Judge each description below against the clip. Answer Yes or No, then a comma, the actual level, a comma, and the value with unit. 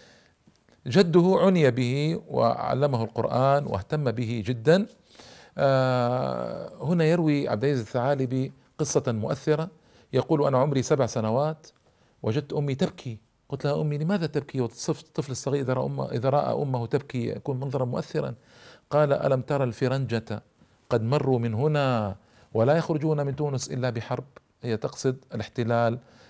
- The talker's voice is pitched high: No, low, 135 Hz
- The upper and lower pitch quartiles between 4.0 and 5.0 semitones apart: No, average, 3.6 semitones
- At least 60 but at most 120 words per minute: No, average, 130 wpm